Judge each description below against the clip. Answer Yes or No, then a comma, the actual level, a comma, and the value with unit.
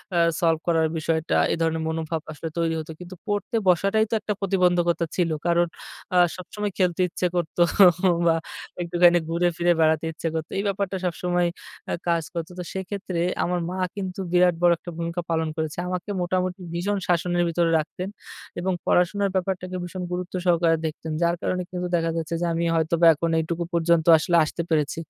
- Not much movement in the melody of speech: Yes, narrow, 1.8 semitones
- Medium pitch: Yes, medium, 175 Hz